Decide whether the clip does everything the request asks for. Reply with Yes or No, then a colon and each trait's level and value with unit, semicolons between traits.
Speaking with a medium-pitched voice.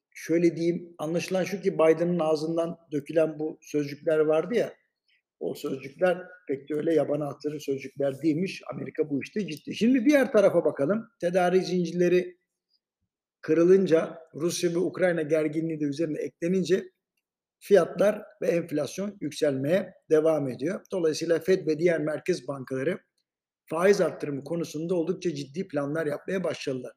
Yes: medium, 165 Hz